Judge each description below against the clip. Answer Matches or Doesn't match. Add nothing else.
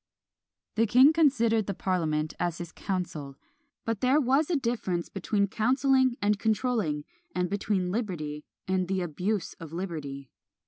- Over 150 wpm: Doesn't match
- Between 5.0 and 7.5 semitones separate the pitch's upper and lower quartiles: Matches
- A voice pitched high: Matches